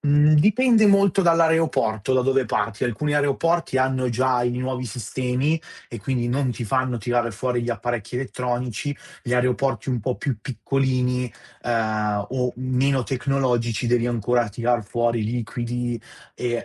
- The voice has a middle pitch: No, low, 125 Hz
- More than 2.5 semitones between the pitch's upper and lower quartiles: No, narrow, 2.2 semitones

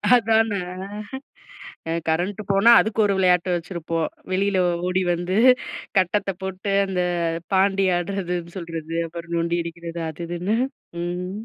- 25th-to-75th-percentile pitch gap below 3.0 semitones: Yes, narrow, 2.5 semitones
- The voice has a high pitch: No, medium, 180 Hz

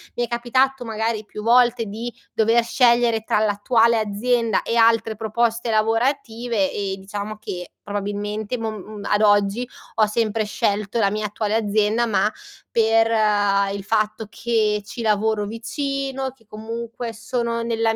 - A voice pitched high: Yes, high, 225 Hz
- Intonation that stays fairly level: Yes, narrow, 2.0 semitones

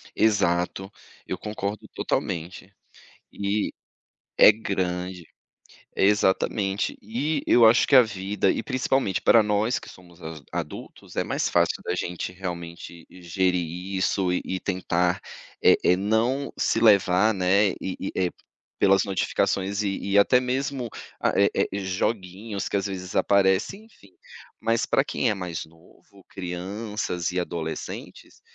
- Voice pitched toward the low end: Yes, very low, 95 Hz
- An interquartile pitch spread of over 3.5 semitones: No, average, 3.0 semitones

